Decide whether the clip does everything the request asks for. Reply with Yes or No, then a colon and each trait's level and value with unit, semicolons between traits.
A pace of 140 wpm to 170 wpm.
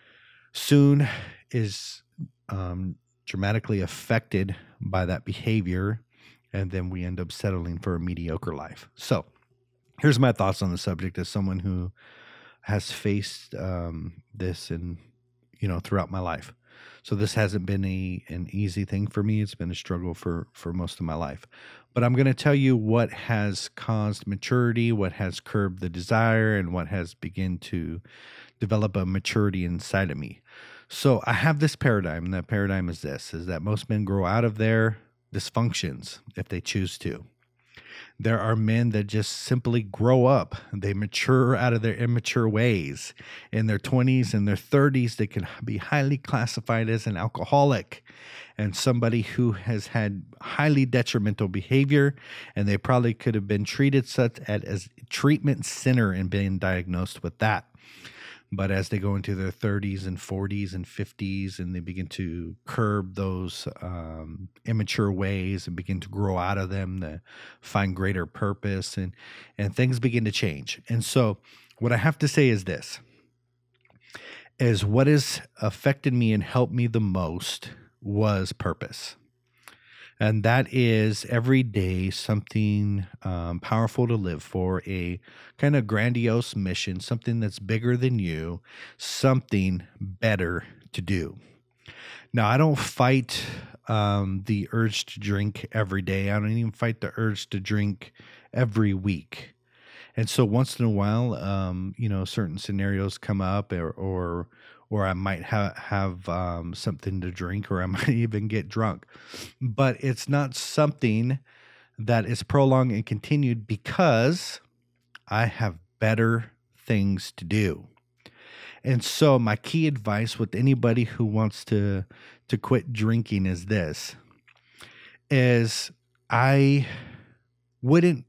Yes: average, 155 wpm